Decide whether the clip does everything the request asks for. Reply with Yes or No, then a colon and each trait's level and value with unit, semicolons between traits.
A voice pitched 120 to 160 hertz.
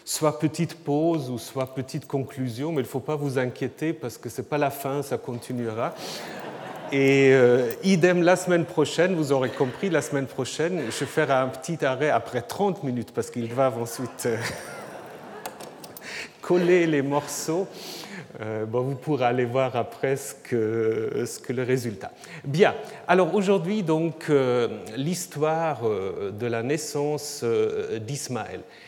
Yes: medium, 140 Hz